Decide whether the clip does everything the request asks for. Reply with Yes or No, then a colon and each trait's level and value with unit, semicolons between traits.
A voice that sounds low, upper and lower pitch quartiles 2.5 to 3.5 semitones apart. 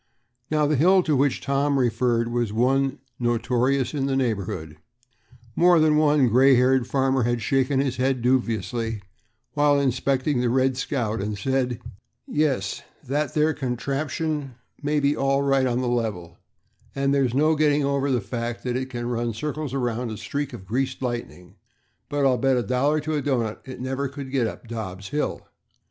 Yes: low, 130 Hz; average, 2.9 semitones